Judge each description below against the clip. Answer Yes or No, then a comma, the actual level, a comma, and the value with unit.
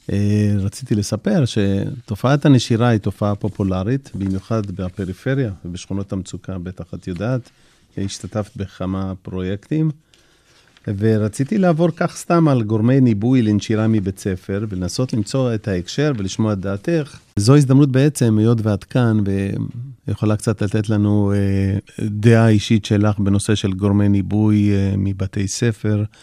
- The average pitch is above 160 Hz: No, low, 105 Hz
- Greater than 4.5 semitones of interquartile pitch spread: No, average, 3.8 semitones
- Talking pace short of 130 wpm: Yes, average, 120 wpm